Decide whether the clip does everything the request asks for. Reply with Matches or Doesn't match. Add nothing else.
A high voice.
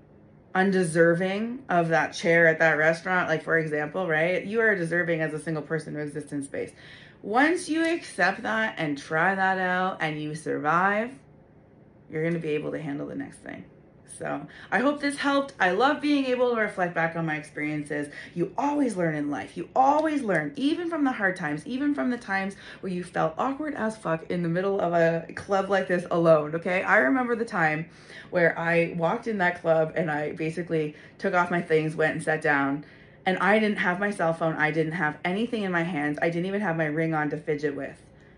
Doesn't match